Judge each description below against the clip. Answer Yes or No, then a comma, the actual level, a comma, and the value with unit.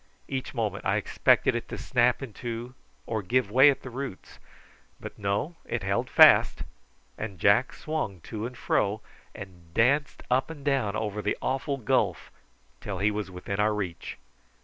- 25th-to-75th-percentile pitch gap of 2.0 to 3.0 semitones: No, average, 4.5 semitones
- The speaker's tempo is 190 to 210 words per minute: No, average, 170 wpm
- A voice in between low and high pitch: No, low, 110 Hz